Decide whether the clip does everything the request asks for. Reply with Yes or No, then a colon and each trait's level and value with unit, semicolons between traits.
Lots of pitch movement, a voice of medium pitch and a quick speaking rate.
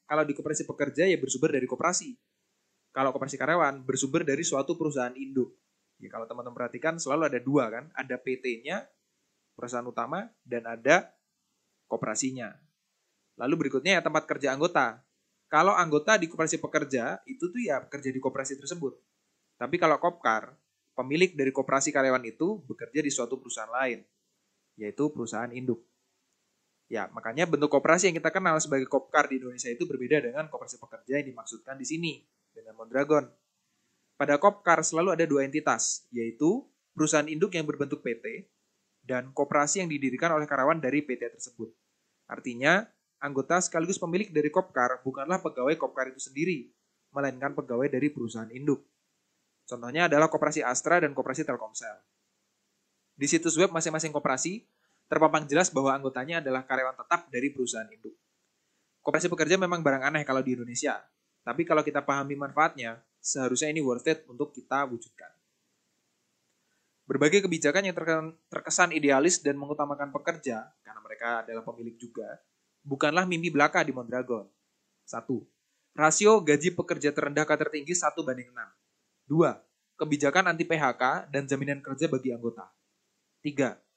No: average, 3.9 semitones; medium, 145 Hz; fast, 145 wpm